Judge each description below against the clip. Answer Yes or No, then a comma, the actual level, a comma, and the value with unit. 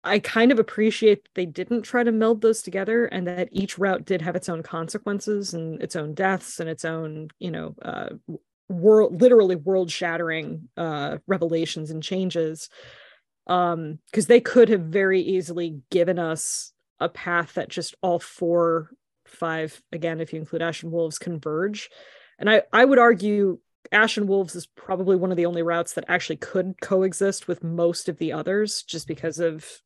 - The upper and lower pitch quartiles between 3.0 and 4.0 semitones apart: Yes, average, 3.6 semitones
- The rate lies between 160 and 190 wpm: Yes, average, 175 wpm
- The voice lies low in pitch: No, medium, 180 Hz